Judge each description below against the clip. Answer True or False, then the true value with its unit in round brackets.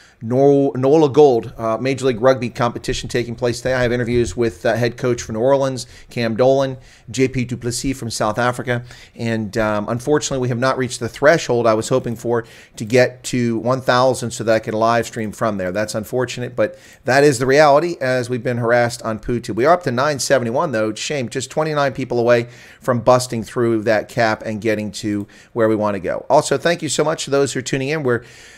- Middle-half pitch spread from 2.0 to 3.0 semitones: True (2.4 semitones)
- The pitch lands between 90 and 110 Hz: False (120 Hz)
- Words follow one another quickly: True (215 wpm)